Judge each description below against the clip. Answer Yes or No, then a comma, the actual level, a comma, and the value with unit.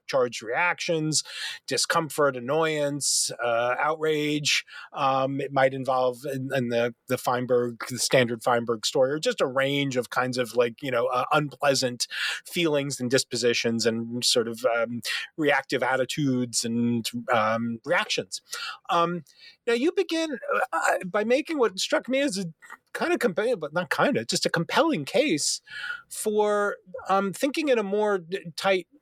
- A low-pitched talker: No, medium, 145 Hz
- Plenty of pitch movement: Yes, wide, 7.9 semitones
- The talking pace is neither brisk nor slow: Yes, average, 150 wpm